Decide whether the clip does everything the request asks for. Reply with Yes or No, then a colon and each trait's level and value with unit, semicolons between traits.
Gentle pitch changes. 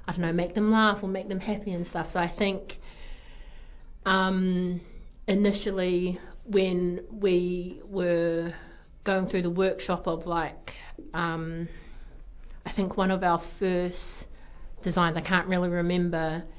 Yes: narrow, 1.7 semitones